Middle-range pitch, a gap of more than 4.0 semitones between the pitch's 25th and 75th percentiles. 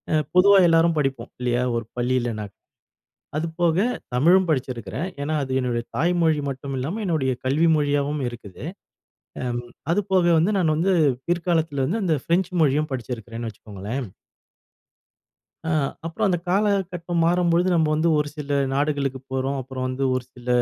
Yes: medium, 150 Hz; average, 5.0 semitones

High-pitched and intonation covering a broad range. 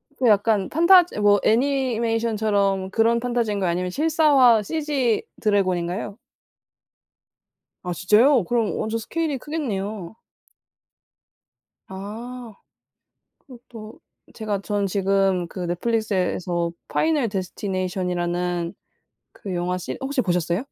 No: high, 210 Hz; average, 4.5 semitones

